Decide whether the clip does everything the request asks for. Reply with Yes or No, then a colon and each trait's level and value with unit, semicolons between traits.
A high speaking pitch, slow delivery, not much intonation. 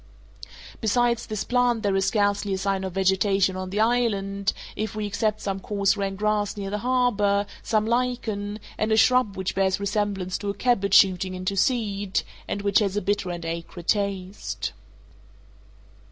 No: high, 200 Hz; average, 170 wpm; narrow, 1.9 semitones